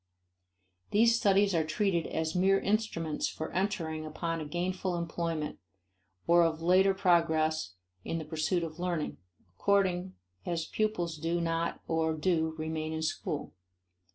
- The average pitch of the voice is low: No, medium, 170 Hz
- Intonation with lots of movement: No, average, 2.7 semitones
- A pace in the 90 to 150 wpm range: Yes, slow, 135 wpm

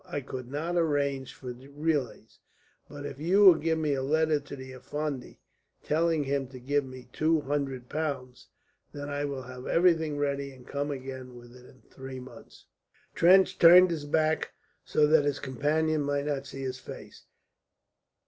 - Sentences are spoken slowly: No, average, 165 wpm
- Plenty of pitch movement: No, average, 2.9 semitones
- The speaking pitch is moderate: Yes, medium, 145 Hz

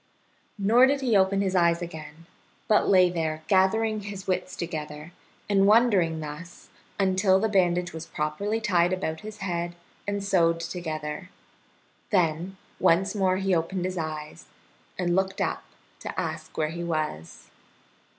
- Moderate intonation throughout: Yes, average, 3.2 semitones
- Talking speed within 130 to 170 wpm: Yes, average, 145 wpm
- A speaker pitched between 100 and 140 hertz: No, medium, 180 Hz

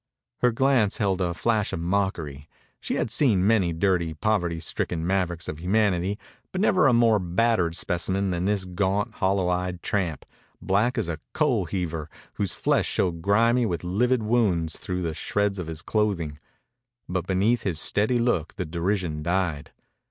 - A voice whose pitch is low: Yes, very low, 95 Hz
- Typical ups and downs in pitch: Yes, average, 3.8 semitones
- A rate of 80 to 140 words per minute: No, average, 165 wpm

